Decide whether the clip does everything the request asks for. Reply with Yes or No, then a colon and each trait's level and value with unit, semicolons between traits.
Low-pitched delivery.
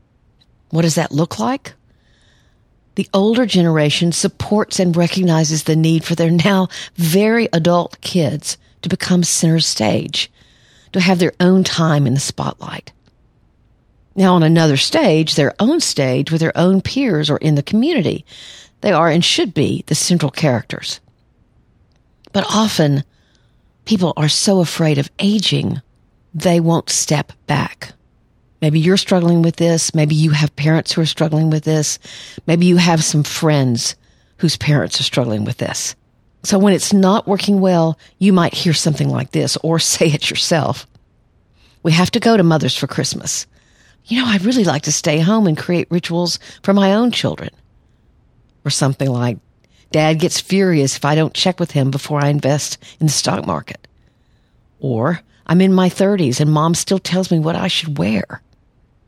No: medium, 165 Hz